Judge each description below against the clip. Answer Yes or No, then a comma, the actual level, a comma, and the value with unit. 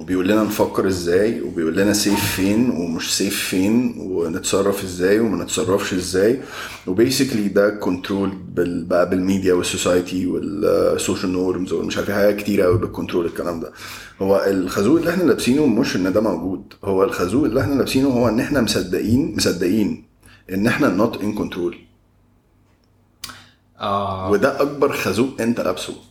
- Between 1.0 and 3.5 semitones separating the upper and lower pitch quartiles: Yes, narrow, 2.5 semitones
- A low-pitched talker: Yes, low, 100 Hz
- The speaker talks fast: Yes, fast, 140 wpm